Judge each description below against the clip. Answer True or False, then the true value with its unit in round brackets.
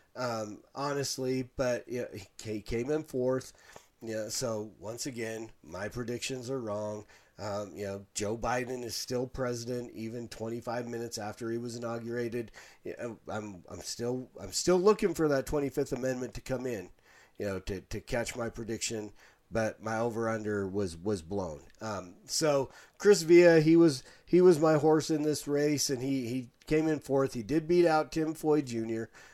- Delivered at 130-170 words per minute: False (180 wpm)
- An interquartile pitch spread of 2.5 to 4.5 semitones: True (4.1 semitones)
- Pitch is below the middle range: True (120 Hz)